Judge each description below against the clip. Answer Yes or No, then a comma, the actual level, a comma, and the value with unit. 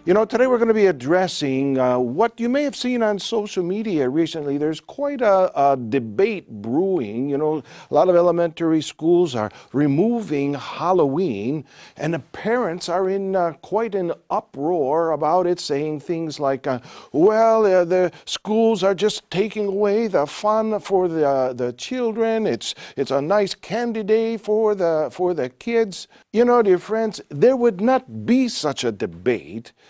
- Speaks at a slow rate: No, average, 175 wpm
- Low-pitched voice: No, medium, 185 Hz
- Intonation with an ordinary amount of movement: No, wide, 6.7 semitones